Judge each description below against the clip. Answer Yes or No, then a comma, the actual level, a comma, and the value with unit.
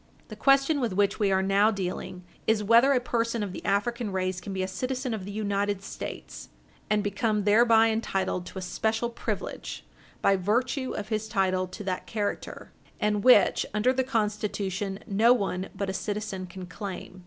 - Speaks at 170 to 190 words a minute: Yes, average, 180 wpm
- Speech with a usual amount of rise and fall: Yes, average, 3.0 semitones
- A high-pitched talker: Yes, high, 205 Hz